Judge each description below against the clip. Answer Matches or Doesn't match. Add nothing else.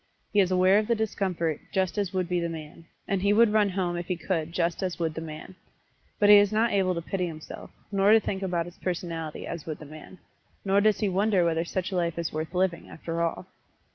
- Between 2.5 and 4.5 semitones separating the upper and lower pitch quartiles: Matches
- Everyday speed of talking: Doesn't match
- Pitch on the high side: Doesn't match